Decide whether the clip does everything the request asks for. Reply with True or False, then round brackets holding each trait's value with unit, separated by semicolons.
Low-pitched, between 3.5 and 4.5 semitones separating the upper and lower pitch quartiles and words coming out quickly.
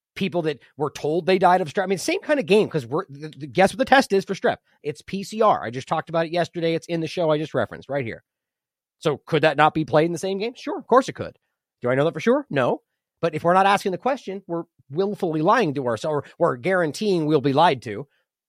False (170 Hz; 4.2 semitones; 265 wpm)